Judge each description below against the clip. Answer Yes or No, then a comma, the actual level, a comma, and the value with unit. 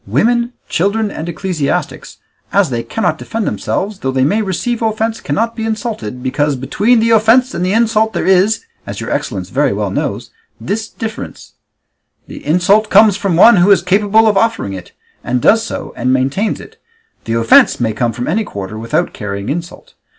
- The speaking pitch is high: Yes, high, 195 Hz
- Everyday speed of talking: Yes, average, 180 wpm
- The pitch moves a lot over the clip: Yes, wide, 8.8 semitones